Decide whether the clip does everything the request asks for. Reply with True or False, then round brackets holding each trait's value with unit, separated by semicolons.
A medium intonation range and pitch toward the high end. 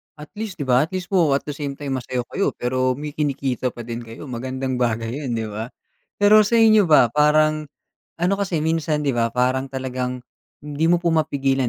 False (4.0 semitones; 140 Hz)